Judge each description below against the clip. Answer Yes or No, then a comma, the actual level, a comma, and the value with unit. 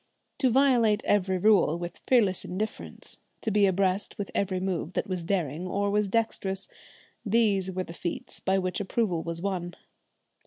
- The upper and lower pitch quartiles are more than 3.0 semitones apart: No, narrow, 2.5 semitones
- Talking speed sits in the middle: Yes, average, 160 wpm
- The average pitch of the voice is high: Yes, high, 195 Hz